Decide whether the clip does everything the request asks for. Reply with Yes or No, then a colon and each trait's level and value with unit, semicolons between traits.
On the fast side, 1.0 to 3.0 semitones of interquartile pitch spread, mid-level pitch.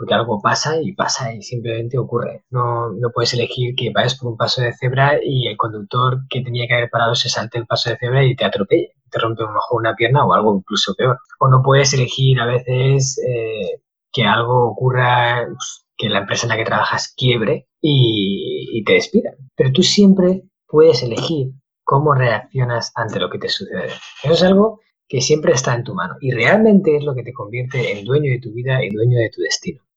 No: fast, 215 wpm; average, 2.7 semitones; low, 125 Hz